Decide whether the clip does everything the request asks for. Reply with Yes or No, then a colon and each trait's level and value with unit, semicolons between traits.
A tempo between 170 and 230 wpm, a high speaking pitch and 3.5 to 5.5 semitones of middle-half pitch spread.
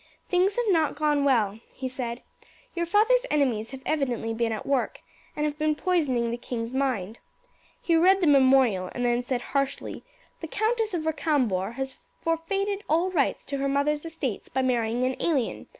Yes: average, 175 wpm; very high, 275 Hz; average, 5.2 semitones